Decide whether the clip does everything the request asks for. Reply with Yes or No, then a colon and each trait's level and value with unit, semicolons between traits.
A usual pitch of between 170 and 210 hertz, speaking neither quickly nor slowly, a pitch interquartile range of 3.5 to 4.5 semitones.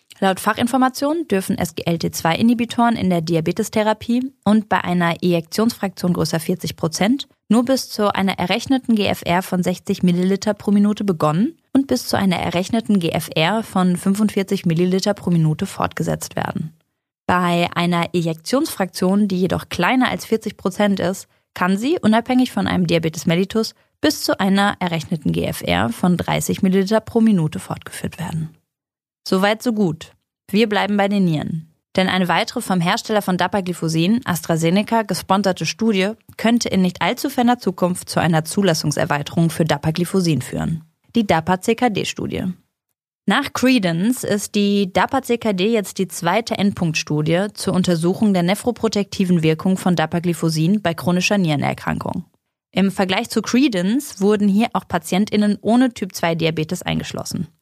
Yes: high, 190 Hz; average, 135 wpm; average, 3.9 semitones